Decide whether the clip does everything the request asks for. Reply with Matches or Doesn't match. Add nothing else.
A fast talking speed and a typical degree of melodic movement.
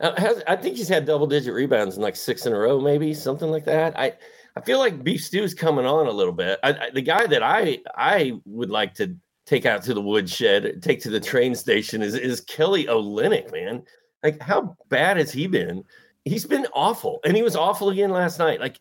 Doesn't match